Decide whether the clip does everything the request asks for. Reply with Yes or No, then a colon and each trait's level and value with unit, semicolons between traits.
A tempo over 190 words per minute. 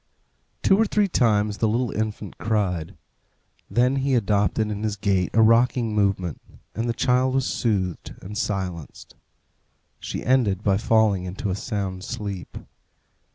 No: average, 145 wpm